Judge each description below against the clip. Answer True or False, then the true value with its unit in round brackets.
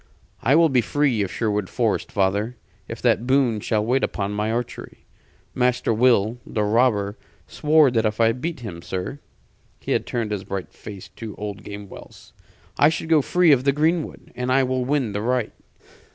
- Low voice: True (115 Hz)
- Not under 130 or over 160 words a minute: False (180 wpm)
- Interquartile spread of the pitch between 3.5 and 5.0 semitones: True (4.1 semitones)